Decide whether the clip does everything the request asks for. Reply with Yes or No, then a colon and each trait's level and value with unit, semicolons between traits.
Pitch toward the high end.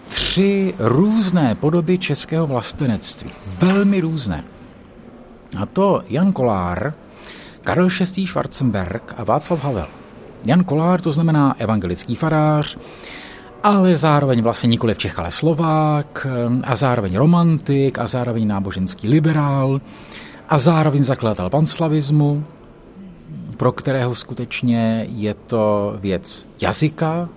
No: medium, 140 Hz